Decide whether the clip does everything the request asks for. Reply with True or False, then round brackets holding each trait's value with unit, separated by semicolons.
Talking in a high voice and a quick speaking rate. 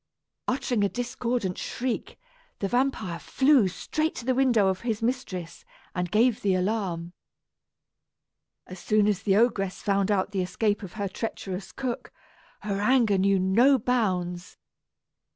False (205 Hz; 140 wpm)